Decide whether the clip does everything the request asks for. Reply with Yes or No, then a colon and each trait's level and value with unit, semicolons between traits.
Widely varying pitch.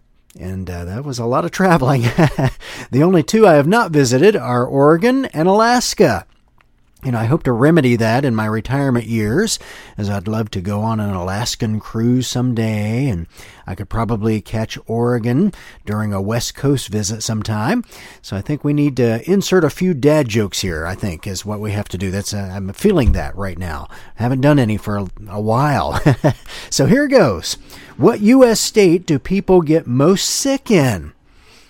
Yes: wide, 6.1 semitones